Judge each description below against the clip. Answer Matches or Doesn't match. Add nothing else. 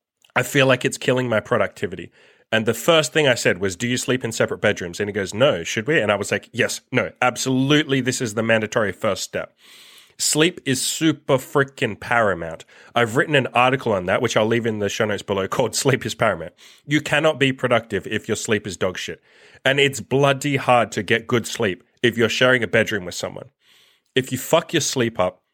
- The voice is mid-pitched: Doesn't match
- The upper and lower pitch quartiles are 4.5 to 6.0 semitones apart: Doesn't match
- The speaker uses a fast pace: Matches